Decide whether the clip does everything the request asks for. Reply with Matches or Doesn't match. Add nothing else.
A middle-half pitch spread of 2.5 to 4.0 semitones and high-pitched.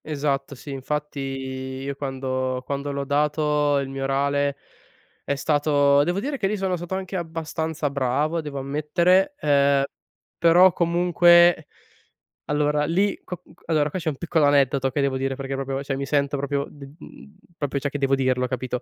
Doesn't match